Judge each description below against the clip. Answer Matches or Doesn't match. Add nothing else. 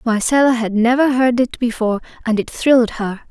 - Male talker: Doesn't match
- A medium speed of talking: Matches